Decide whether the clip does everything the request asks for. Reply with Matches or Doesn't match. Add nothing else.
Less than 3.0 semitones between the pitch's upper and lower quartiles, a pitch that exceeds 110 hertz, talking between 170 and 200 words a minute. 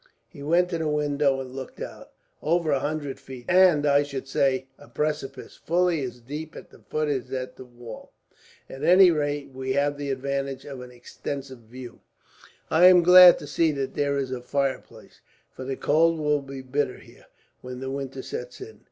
Matches